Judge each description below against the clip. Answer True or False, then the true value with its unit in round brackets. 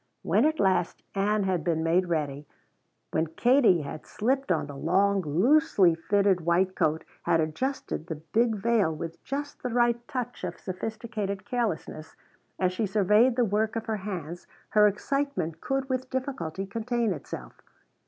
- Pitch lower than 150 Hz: False (200 Hz)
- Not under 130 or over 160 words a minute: True (155 wpm)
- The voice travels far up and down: True (6.0 semitones)